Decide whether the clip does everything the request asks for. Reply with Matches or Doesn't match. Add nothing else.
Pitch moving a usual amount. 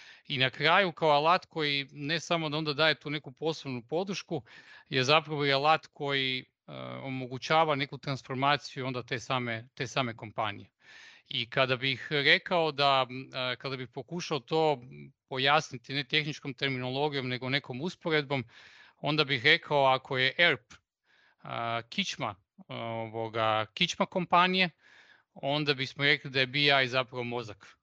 Matches